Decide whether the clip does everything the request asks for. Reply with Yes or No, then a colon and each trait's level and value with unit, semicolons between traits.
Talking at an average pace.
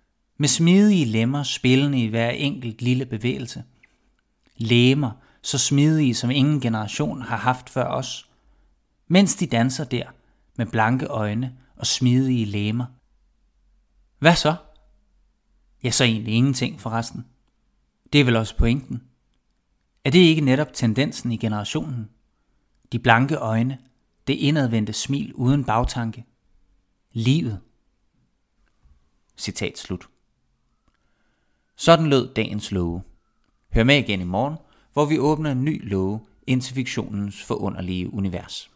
No: slow, 120 wpm